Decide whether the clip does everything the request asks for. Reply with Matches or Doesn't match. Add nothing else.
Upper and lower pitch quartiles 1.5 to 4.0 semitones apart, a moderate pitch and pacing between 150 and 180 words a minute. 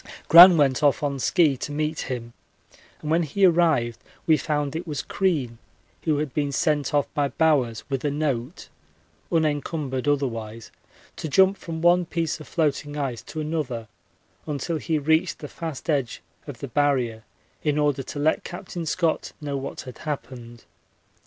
Matches